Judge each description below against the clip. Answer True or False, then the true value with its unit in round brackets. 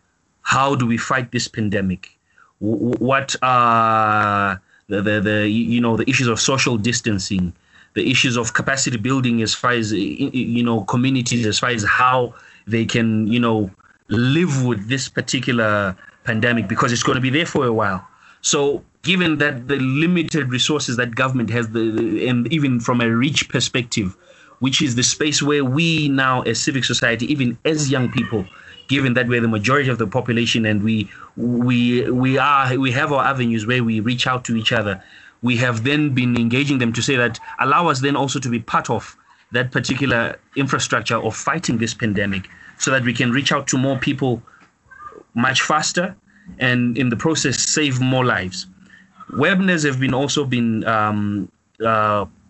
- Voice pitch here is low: True (125 Hz)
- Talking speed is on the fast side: False (175 wpm)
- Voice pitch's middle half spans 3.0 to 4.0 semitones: True (3.4 semitones)